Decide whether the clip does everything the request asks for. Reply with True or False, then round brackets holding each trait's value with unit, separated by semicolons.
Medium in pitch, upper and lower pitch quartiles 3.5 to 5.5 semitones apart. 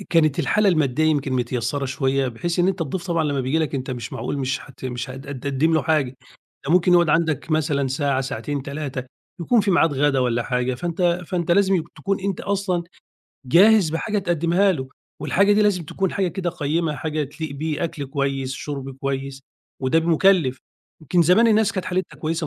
True (155 Hz; 4.6 semitones)